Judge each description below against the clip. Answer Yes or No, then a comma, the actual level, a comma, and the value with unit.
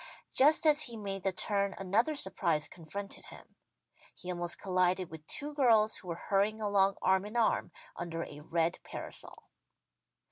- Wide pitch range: No, average, 3.8 semitones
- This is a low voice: No, high, 195 Hz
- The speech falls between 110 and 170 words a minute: Yes, average, 155 wpm